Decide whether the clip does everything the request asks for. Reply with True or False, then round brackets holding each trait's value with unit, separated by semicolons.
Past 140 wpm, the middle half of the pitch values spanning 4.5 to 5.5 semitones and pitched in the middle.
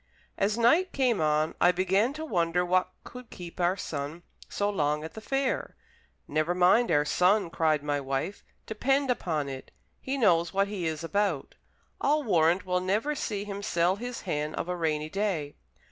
True (175 wpm; 5.1 semitones; 180 Hz)